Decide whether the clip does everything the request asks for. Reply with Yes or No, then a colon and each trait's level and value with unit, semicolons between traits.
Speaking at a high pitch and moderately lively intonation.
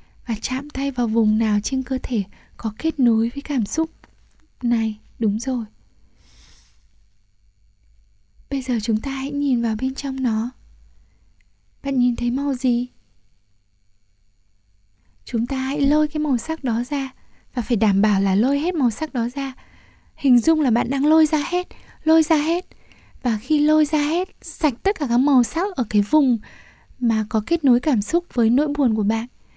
Yes: very high, 250 Hz; average, 4.3 semitones